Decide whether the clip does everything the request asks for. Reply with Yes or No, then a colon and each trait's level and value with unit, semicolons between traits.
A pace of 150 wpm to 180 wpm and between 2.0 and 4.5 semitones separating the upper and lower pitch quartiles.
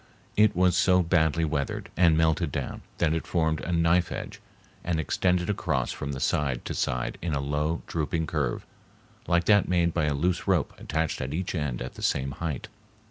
No: average, 190 wpm; average, 2.9 semitones